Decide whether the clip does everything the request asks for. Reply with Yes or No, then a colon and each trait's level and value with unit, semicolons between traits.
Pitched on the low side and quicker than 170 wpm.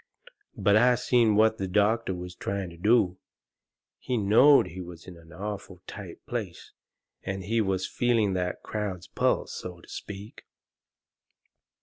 No: low, 100 Hz; average, 145 wpm